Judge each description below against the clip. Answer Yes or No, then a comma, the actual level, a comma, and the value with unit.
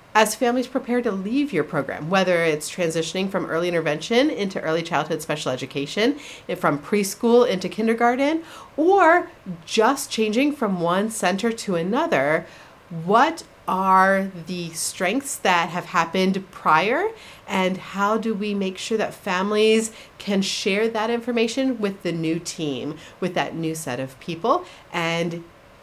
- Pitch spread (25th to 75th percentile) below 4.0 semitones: No, average, 5.2 semitones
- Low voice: No, high, 190 Hz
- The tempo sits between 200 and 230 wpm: No, average, 140 wpm